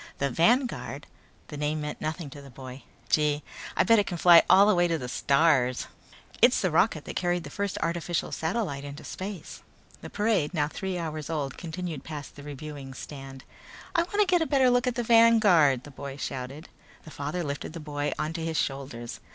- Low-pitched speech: No, medium, 160 Hz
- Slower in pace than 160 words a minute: No, average, 195 wpm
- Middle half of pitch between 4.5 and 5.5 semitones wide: Yes, average, 4.8 semitones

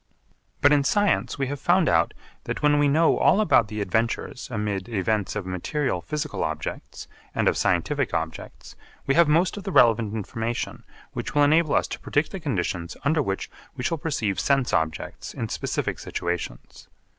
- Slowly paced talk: No, average, 175 wpm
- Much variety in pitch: Yes, wide, 6.8 semitones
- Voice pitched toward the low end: Yes, low, 125 Hz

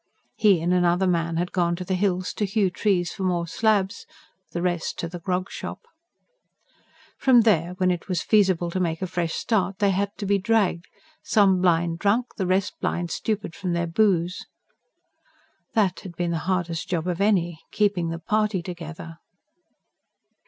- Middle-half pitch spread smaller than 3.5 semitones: Yes, narrow, 2.6 semitones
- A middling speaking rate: Yes, average, 175 wpm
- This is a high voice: No, medium, 180 Hz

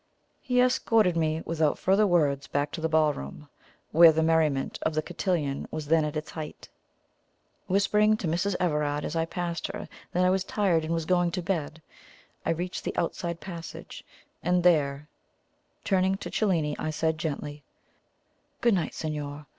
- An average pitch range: Yes, average, 3.1 semitones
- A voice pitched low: No, medium, 165 Hz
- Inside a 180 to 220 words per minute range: No, average, 165 wpm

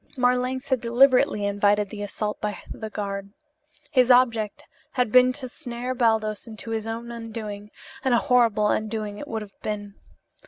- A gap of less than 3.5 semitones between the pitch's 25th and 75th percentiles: Yes, average, 3.0 semitones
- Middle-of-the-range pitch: No, high, 225 Hz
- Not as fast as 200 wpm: Yes, average, 160 wpm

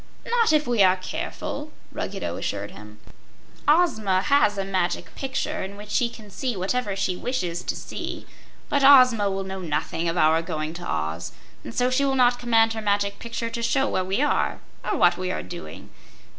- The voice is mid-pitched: No, high, 200 Hz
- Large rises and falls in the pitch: Yes, wide, 5.9 semitones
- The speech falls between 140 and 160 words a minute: No, average, 190 wpm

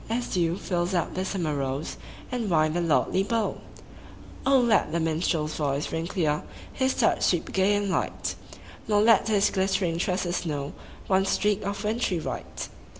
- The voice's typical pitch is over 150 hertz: Yes, medium, 185 Hz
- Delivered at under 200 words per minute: Yes, average, 160 wpm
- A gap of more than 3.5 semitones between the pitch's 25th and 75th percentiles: Yes, average, 4.2 semitones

